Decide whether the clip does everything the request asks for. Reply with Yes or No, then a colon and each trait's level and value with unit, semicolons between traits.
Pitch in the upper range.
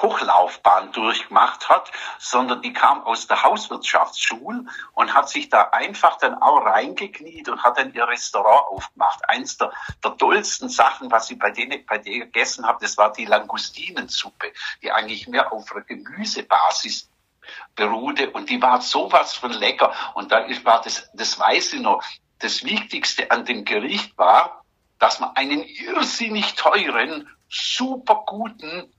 Yes: high, 235 Hz